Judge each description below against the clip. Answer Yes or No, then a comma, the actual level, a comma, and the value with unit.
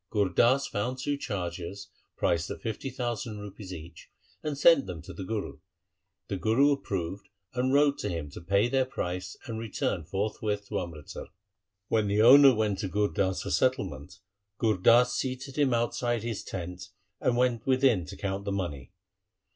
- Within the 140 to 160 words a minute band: No, average, 170 wpm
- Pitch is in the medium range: No, low, 105 Hz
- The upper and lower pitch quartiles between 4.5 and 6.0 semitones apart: Yes, average, 5.3 semitones